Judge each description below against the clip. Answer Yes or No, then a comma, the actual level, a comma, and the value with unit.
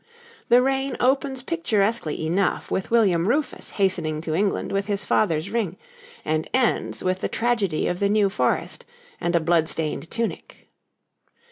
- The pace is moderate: Yes, average, 150 wpm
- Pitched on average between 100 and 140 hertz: No, high, 200 Hz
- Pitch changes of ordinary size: No, wide, 5.7 semitones